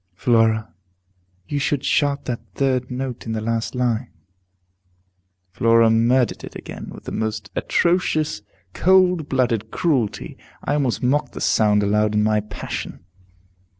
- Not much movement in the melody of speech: No, average, 4.2 semitones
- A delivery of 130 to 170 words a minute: Yes, slow, 135 wpm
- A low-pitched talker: Yes, low, 120 Hz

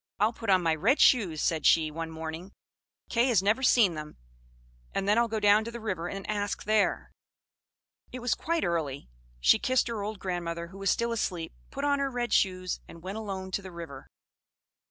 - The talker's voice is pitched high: Yes, high, 195 Hz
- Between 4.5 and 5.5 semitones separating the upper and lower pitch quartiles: Yes, average, 5.2 semitones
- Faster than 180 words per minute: Yes, average, 200 wpm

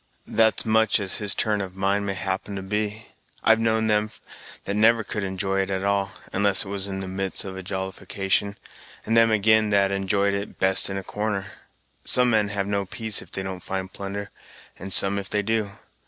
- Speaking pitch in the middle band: No, low, 100 Hz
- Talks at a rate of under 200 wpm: No, fast, 205 wpm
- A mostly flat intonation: Yes, narrow, 1.8 semitones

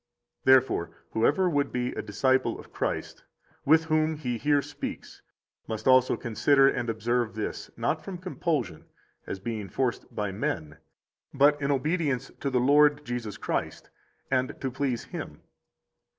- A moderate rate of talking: Yes, average, 145 wpm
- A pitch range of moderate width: Yes, average, 4.0 semitones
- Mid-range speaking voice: No, low, 130 Hz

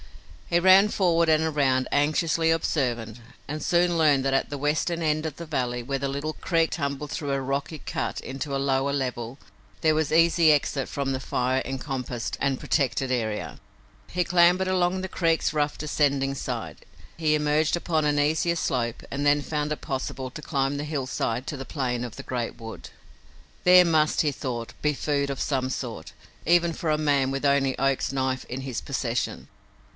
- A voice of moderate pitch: Yes, medium, 145 Hz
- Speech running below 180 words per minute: No, average, 185 wpm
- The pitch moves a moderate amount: Yes, average, 3.1 semitones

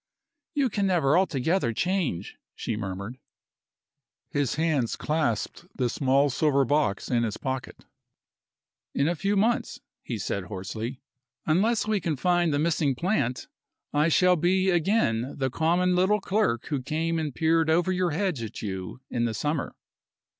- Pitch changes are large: Yes, wide, 6.3 semitones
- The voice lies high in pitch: No, medium, 155 Hz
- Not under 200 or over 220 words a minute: No, average, 150 wpm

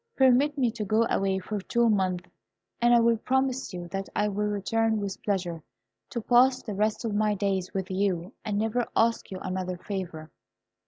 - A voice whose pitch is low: No, high, 210 Hz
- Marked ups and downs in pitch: No, average, 3.5 semitones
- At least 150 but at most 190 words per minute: Yes, average, 180 wpm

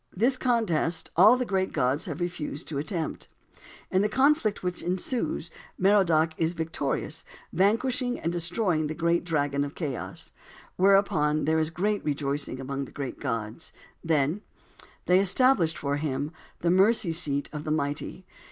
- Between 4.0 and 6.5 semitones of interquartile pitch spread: Yes, average, 4.7 semitones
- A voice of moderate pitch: Yes, medium, 165 Hz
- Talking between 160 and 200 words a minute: No, average, 150 wpm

